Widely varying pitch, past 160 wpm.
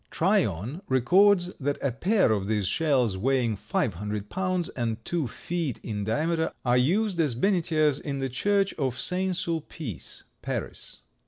No: wide, 7.2 semitones; average, 150 wpm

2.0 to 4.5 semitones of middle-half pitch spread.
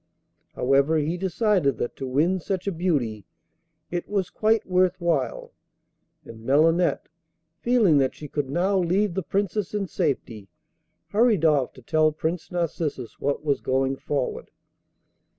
No: average, 5.3 semitones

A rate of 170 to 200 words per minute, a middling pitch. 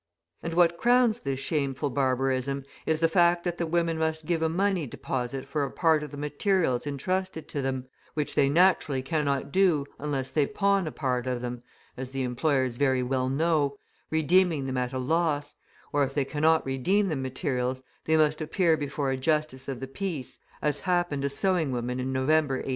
Yes: average, 190 wpm; medium, 145 Hz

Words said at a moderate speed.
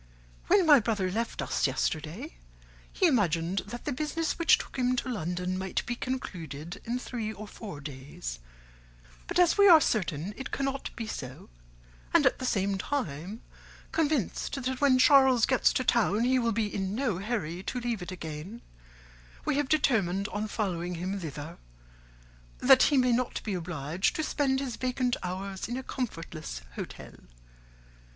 Yes: average, 165 wpm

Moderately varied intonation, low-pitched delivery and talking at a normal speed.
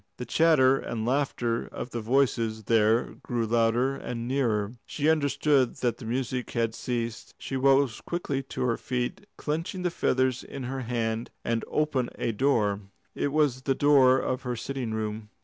Yes: average, 3.0 semitones; low, 125 Hz; average, 165 wpm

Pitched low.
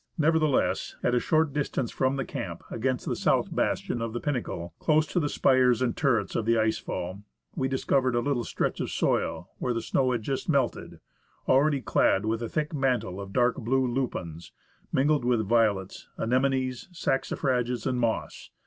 Yes: low, 125 Hz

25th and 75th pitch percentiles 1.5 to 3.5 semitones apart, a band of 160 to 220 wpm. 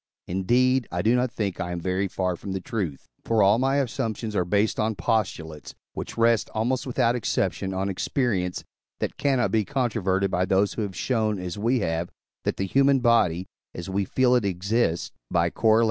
No: average, 4.5 semitones; average, 185 wpm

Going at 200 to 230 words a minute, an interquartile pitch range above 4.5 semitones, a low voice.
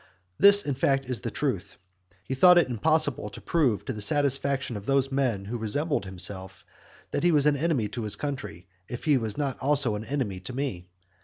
Yes: fast, 205 wpm; wide, 5.5 semitones; low, 130 Hz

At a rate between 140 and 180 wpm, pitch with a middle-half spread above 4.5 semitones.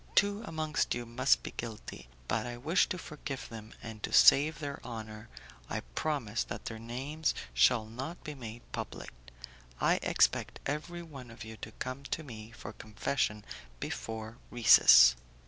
Yes: average, 160 wpm; average, 5.1 semitones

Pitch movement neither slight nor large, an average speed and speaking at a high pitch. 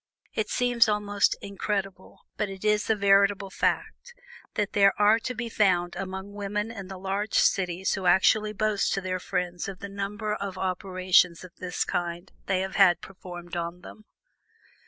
No: narrow, 2.1 semitones; average, 170 wpm; high, 195 Hz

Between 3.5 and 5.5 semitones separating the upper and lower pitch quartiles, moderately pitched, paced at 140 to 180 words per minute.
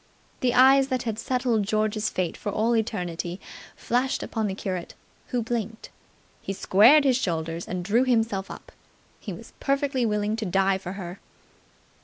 No: average, 4.2 semitones; high, 215 Hz; average, 160 wpm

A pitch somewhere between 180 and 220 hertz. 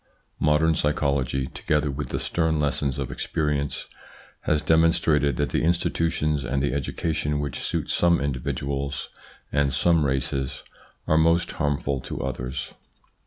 No: very low, 75 Hz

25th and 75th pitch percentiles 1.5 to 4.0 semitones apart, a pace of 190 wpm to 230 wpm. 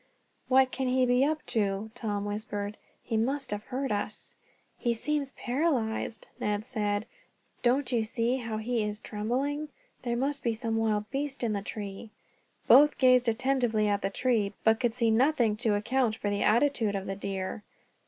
No: average, 3.7 semitones; average, 175 wpm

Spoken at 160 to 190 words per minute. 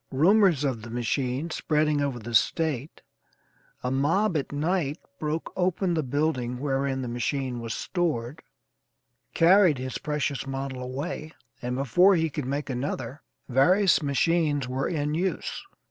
No: average, 140 wpm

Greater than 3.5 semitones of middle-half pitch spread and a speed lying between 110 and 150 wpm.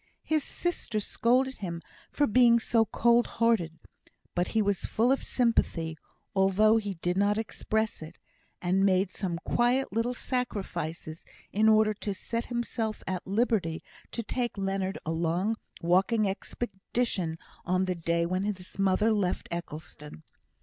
Yes: average, 4.4 semitones; average, 145 wpm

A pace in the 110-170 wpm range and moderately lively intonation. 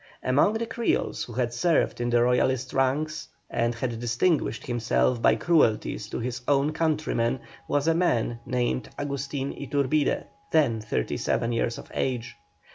Yes: average, 150 wpm; average, 3.7 semitones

